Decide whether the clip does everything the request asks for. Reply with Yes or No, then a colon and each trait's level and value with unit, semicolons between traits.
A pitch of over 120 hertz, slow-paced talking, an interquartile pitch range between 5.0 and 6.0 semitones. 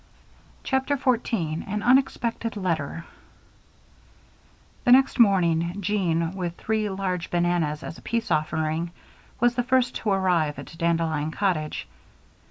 Yes: medium, 185 Hz; slow, 120 wpm; wide, 5.6 semitones